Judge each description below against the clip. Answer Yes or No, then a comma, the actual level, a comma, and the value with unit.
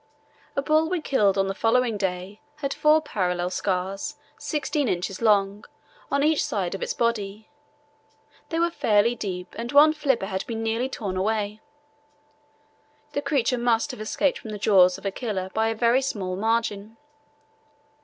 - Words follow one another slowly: No, average, 165 wpm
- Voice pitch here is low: No, high, 220 Hz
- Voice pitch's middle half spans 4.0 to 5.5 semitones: Yes, average, 5.1 semitones